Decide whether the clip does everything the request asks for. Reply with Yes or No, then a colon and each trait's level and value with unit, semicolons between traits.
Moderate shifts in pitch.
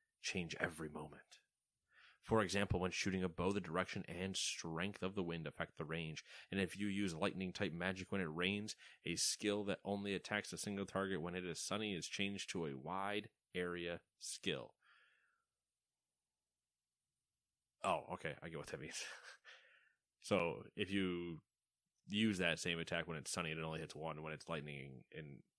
Yes: average, 3.5 semitones